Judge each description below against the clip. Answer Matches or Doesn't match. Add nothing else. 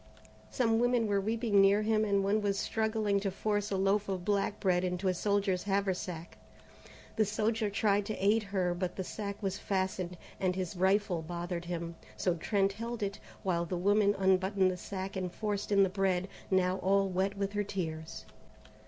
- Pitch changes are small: Matches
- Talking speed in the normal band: Matches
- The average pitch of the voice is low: Doesn't match